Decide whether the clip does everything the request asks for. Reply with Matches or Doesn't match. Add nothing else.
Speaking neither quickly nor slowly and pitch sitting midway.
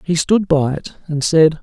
Doesn't match